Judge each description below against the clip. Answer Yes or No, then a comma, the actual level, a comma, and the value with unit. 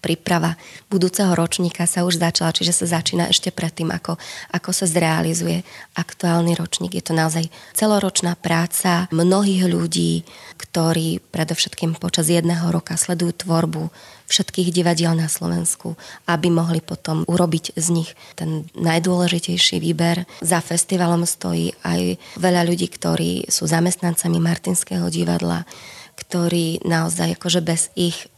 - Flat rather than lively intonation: Yes, narrow, 1.5 semitones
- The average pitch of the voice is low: No, medium, 170 Hz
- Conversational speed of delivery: Yes, average, 130 wpm